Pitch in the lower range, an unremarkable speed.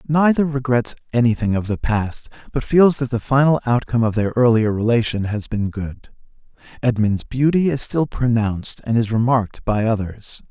Yes: low, 120 Hz; average, 165 wpm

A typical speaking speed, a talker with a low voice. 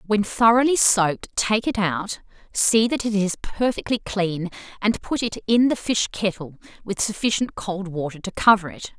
No: average, 175 wpm; high, 205 Hz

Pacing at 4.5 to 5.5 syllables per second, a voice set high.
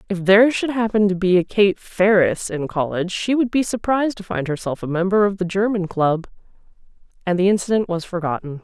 No: 5.8 syllables/s; high, 195 Hz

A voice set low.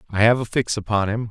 Yes: low, 110 Hz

